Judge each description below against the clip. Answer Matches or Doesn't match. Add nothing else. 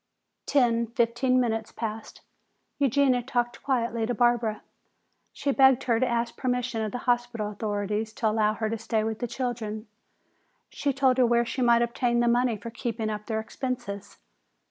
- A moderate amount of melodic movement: Doesn't match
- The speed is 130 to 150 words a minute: Doesn't match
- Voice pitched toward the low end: Doesn't match